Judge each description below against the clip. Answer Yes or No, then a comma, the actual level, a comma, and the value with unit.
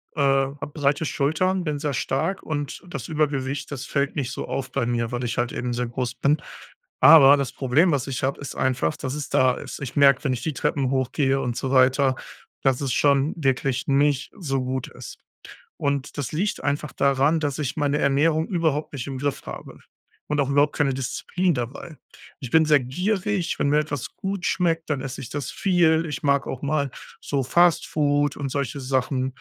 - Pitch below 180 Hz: Yes, medium, 140 Hz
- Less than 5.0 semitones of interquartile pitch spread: Yes, narrow, 2.4 semitones